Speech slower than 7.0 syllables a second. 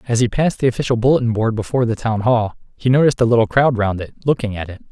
No: 7.4 syllables/s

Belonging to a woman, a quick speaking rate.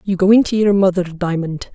Yes: female; fast, 240 wpm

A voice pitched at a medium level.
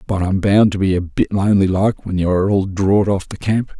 No: very low, 95 Hz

